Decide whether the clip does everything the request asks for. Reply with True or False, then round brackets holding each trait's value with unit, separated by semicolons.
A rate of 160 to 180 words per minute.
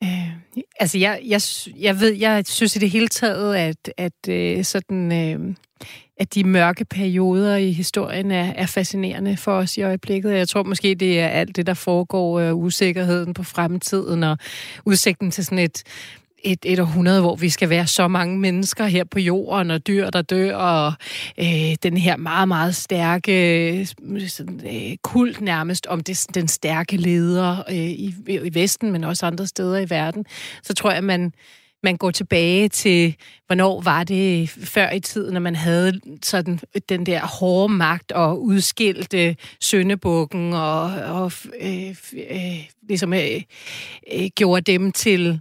True (170 wpm)